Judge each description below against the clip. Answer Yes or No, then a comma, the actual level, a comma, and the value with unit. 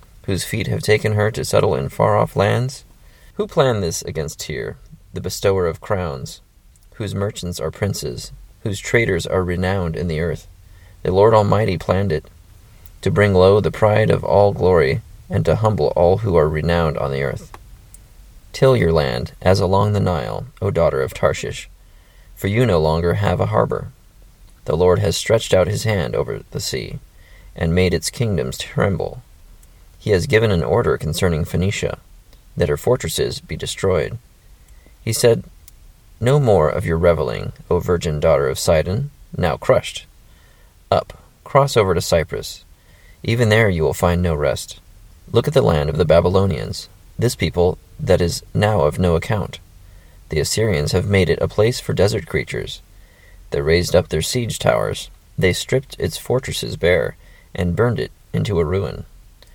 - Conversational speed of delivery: Yes, average, 170 wpm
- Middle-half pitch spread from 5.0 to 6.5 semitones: No, average, 3.8 semitones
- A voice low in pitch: Yes, very low, 90 Hz